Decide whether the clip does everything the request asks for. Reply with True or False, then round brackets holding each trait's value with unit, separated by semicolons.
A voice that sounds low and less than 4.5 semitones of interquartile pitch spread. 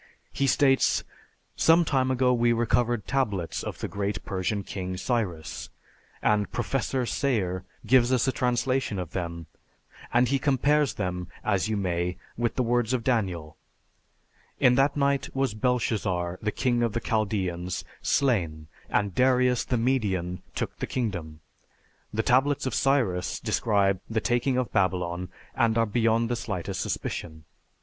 False (115 Hz; 5.5 semitones)